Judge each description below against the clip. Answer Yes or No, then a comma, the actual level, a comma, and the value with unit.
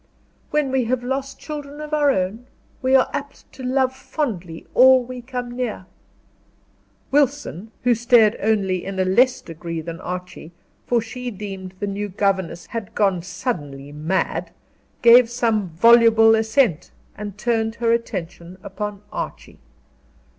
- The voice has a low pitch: No, high, 225 Hz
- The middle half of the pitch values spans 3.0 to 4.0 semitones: No, average, 5.1 semitones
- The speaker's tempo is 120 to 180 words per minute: Yes, average, 140 wpm